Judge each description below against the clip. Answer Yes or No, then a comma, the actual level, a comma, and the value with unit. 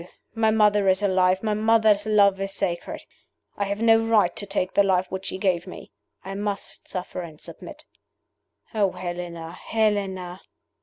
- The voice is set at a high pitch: Yes, high, 195 Hz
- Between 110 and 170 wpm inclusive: Yes, average, 160 wpm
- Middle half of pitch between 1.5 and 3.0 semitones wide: Yes, narrow, 2.4 semitones